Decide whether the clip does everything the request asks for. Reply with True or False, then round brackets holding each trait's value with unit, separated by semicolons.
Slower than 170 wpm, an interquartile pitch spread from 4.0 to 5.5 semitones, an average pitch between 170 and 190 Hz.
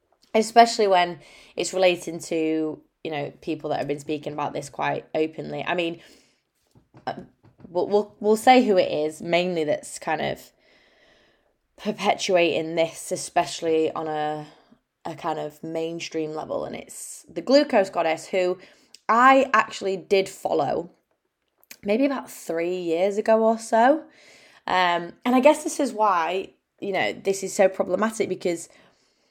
True (145 wpm; 4.9 semitones; 185 Hz)